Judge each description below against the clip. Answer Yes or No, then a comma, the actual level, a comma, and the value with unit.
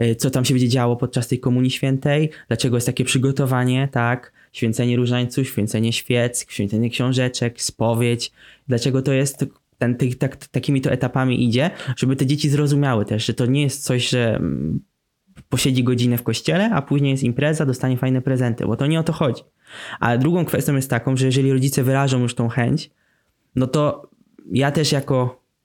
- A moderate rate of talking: No, fast, 180 wpm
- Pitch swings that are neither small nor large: No, narrow, 2.3 semitones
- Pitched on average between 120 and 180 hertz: Yes, low, 130 Hz